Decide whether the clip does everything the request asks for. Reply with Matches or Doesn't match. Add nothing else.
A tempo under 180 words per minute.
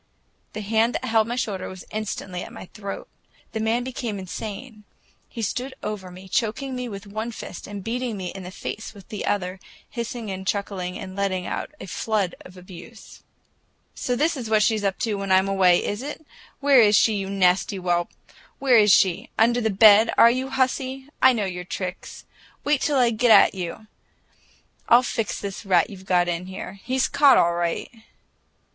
Doesn't match